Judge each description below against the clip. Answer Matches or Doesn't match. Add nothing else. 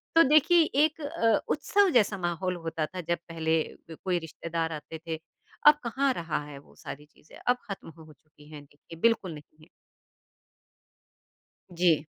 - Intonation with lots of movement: Matches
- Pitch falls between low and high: Matches